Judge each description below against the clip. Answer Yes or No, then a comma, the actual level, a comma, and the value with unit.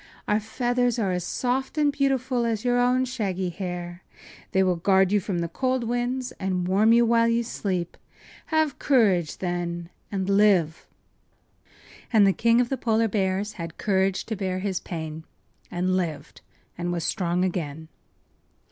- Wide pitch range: No, average, 4.9 semitones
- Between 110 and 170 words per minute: Yes, average, 160 wpm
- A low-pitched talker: No, high, 195 Hz